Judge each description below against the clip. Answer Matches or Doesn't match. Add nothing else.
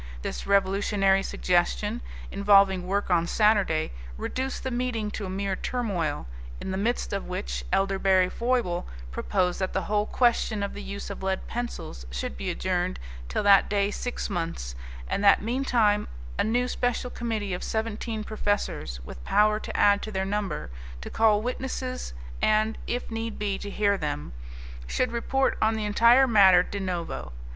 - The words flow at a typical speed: Matches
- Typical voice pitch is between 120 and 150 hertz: Doesn't match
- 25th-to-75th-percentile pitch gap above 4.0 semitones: Doesn't match